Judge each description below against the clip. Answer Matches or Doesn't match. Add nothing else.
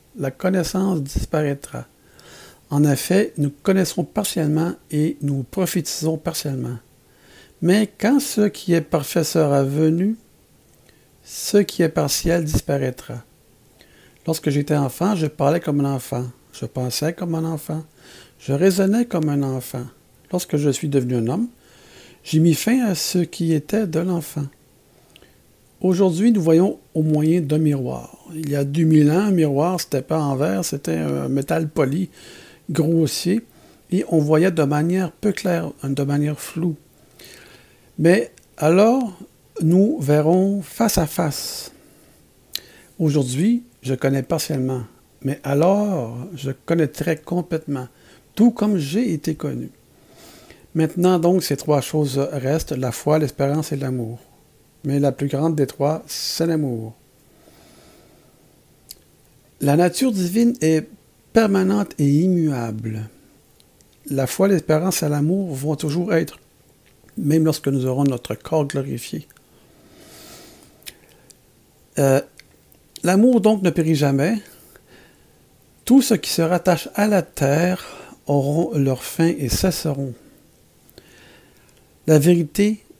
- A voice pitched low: Doesn't match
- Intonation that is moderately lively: Matches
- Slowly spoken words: Matches